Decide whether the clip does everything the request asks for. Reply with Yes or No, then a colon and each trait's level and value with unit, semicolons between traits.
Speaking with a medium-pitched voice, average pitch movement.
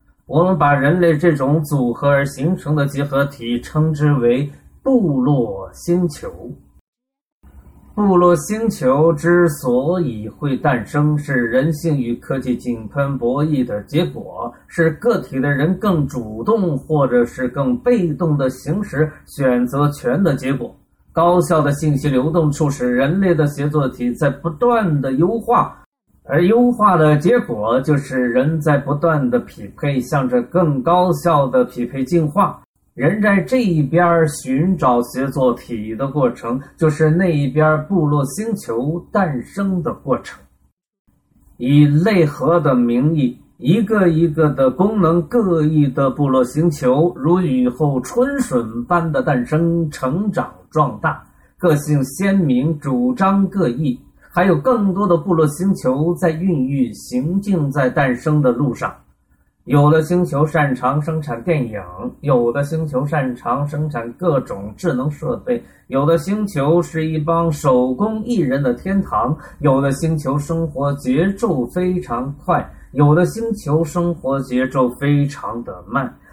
Yes: medium, 150 Hz; average, 4.8 semitones